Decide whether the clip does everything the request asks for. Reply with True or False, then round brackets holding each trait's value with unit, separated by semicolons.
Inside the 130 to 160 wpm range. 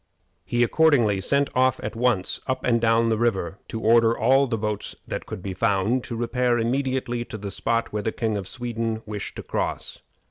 False (200 wpm)